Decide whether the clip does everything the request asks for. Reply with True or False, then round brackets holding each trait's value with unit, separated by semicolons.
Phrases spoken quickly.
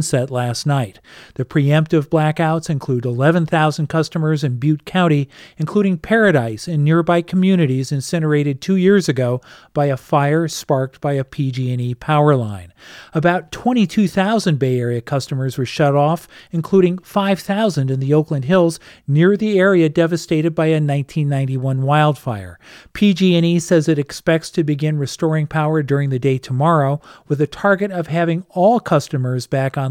False (150 wpm)